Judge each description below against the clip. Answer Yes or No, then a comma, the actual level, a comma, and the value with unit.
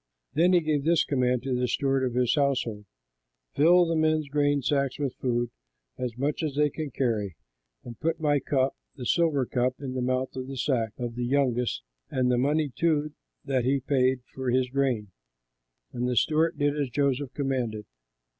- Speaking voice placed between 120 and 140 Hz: Yes, low, 135 Hz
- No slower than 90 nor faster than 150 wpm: No, average, 185 wpm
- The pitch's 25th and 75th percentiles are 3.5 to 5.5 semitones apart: No, average, 2.7 semitones